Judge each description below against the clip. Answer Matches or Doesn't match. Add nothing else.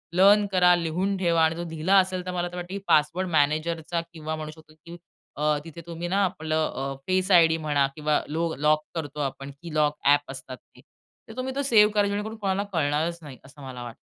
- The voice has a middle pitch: Matches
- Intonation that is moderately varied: Matches